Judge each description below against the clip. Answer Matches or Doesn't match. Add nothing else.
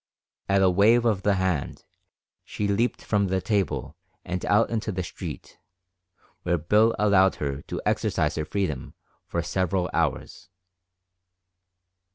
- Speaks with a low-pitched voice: Matches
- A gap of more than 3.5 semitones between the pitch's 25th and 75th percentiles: Doesn't match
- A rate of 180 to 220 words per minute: Doesn't match